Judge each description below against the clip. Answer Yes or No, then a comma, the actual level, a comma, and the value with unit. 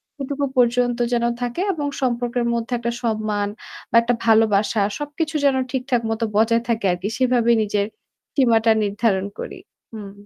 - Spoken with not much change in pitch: Yes, narrow, 2.3 semitones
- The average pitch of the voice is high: Yes, high, 235 Hz